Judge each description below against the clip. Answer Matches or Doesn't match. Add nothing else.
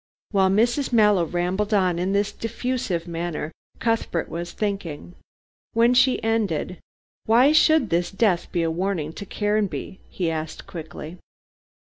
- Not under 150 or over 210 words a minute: Doesn't match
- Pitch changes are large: Doesn't match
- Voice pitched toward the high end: Matches